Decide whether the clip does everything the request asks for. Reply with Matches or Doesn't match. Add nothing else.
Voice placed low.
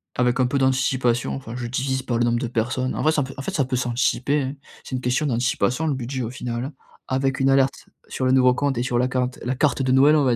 Matches